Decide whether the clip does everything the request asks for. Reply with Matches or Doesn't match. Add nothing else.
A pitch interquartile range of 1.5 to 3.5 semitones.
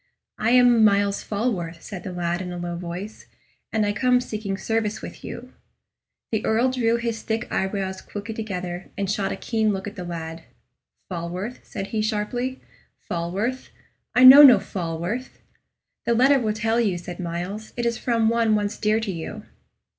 Doesn't match